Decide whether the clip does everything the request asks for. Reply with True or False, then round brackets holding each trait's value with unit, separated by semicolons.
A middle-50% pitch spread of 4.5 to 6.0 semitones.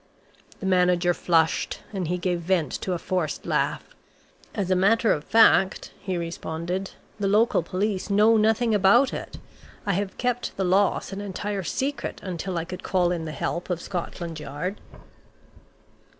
False (2.7 semitones)